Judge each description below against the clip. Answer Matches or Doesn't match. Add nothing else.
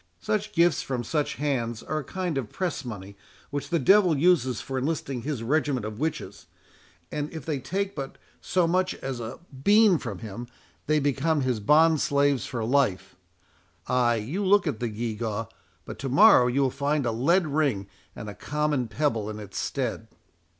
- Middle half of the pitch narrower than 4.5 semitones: Doesn't match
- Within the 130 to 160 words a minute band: Doesn't match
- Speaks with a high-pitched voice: Doesn't match